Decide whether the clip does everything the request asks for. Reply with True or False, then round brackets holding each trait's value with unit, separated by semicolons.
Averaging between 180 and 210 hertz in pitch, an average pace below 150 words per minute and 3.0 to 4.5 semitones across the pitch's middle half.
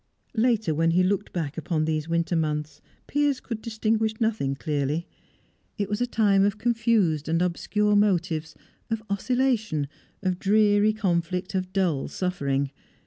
False (190 Hz; 140 wpm; 5.2 semitones)